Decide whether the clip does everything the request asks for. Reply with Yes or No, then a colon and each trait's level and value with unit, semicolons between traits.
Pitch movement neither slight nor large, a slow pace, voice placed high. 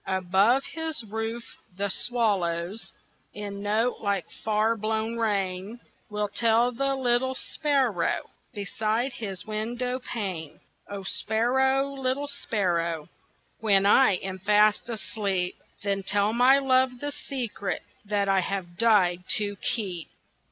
Yes: average, 3.7 semitones; slow, 120 wpm; high, 215 Hz